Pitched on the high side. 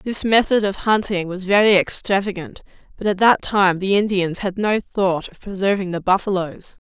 Yes: high, 195 Hz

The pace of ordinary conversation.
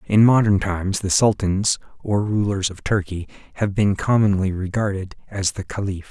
Yes: average, 155 wpm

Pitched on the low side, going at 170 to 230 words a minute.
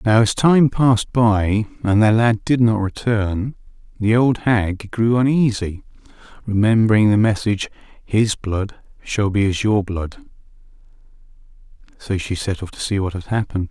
No: low, 105 Hz; average, 155 wpm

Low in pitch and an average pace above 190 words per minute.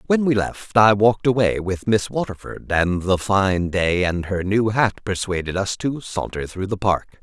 Yes: low, 100 Hz; average, 200 wpm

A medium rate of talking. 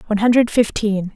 Yes: average, 155 wpm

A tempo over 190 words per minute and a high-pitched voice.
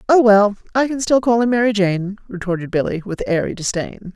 Yes: average, 200 wpm; high, 210 Hz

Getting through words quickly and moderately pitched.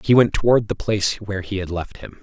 No: fast, 270 wpm; low, 105 Hz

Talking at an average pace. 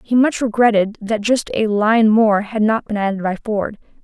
No: fast, 210 wpm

